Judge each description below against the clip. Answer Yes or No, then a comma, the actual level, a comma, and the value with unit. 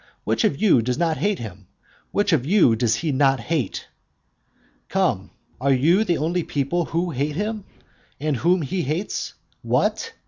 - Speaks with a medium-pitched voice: Yes, medium, 155 Hz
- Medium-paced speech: Yes, average, 165 wpm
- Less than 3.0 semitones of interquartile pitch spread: No, average, 5.1 semitones